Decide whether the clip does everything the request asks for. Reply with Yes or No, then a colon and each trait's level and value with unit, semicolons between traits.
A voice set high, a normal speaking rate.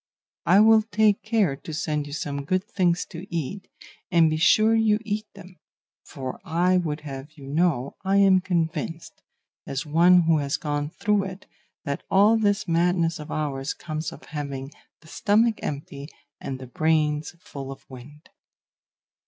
No: medium, 165 Hz; average, 160 wpm